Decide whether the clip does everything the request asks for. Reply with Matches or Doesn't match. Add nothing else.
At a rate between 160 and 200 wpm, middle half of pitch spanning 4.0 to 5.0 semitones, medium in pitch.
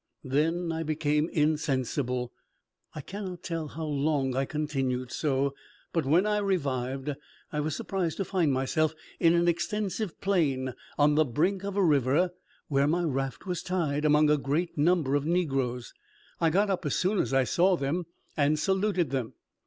Matches